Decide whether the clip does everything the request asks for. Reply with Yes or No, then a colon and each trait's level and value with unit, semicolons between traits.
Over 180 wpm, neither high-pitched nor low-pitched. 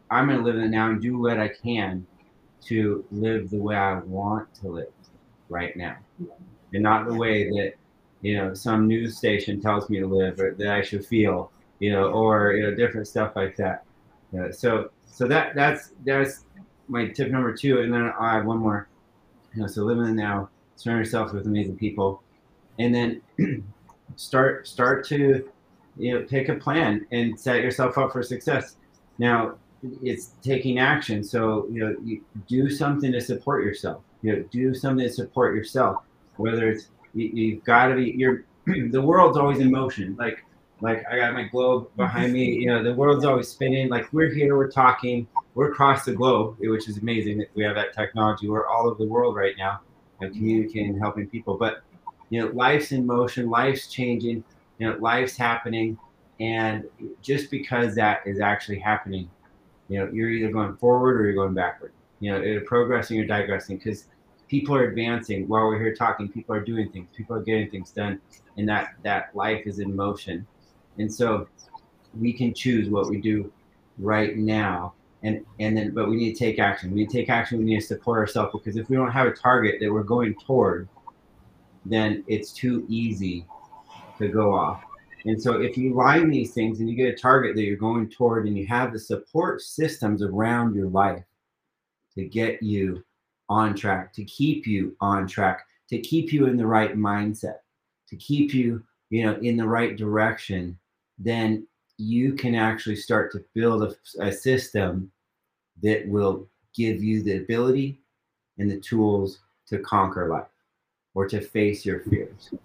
No: average, 190 wpm; low, 110 Hz